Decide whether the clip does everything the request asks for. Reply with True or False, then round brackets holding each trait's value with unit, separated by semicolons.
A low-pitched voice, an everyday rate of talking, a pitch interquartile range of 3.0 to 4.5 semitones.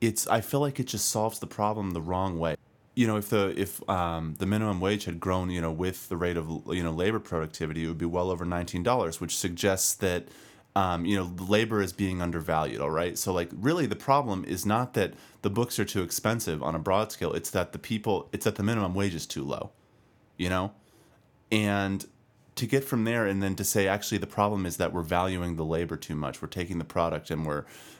False (95 Hz; 235 wpm; 3.8 semitones)